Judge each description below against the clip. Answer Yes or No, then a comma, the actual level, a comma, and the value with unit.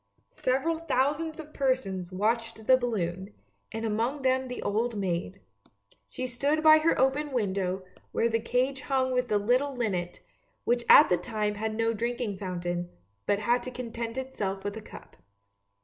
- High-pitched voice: Yes, high, 230 Hz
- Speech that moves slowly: No, average, 165 wpm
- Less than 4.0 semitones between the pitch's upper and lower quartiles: No, average, 4.3 semitones